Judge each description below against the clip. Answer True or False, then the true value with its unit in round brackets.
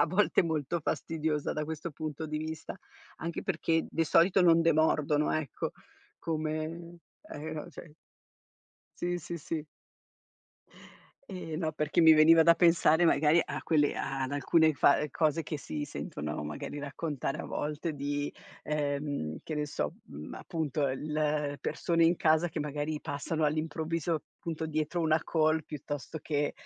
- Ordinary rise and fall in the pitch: False (1.9 semitones)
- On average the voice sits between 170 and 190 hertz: False (155 Hz)